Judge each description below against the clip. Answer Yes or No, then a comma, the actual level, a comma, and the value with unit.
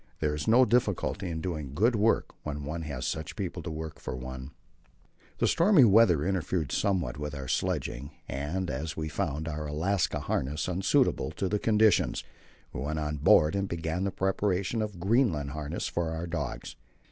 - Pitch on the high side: No, very low, 80 Hz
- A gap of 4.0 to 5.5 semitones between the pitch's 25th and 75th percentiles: Yes, average, 4.7 semitones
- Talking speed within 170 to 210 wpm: Yes, average, 175 wpm